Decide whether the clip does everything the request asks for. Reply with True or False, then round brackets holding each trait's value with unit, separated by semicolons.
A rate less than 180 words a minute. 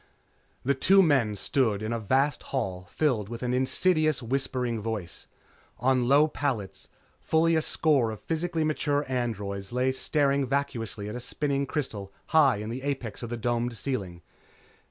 True (155 wpm)